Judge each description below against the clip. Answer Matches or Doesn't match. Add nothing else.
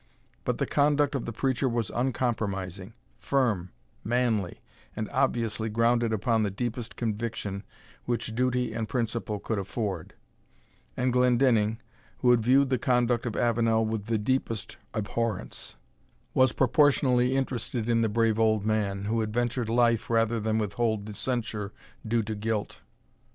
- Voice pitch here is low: Matches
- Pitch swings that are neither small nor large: Doesn't match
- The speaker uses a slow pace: Doesn't match